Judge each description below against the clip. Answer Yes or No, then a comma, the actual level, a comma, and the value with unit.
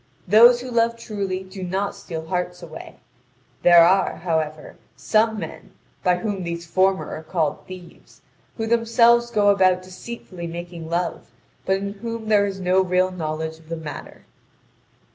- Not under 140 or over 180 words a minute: Yes, average, 155 wpm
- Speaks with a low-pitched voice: No, medium, 185 Hz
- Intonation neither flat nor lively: Yes, average, 3.6 semitones